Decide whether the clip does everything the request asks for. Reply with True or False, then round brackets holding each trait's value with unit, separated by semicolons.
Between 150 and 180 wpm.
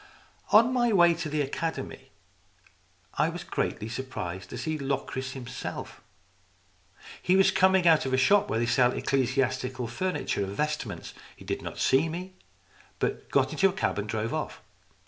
True (165 wpm)